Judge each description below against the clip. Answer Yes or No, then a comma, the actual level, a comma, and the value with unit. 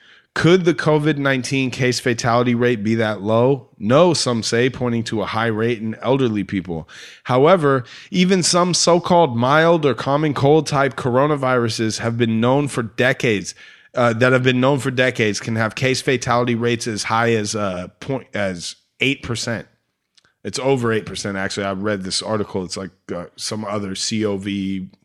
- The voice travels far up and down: No, average, 3.9 semitones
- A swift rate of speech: No, average, 175 wpm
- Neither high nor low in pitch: No, low, 120 Hz